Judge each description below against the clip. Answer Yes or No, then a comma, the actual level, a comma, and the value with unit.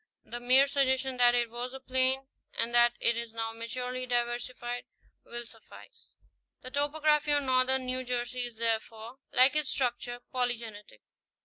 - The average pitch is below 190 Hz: No, very high, 250 Hz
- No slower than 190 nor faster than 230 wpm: No, average, 155 wpm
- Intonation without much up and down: Yes, narrow, 1.6 semitones